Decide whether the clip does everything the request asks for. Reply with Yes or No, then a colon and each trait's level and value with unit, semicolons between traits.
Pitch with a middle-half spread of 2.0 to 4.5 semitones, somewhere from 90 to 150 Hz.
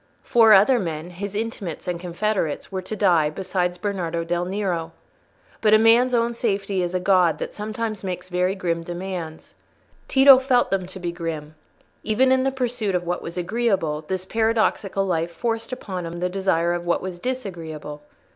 No: average, 4.0 semitones; medium, 185 Hz